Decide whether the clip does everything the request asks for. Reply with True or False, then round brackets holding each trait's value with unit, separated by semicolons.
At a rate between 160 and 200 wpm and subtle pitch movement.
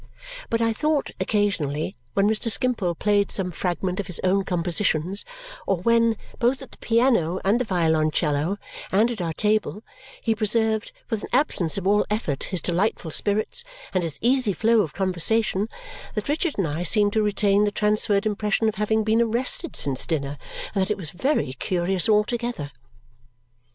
False (170 wpm; 4.0 semitones)